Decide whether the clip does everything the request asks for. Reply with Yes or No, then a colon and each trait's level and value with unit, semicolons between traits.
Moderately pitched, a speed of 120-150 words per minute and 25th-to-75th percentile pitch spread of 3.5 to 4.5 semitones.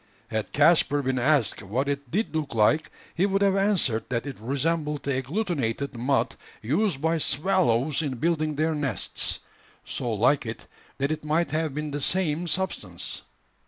No: medium, 145 Hz; average, 160 wpm; average, 4.1 semitones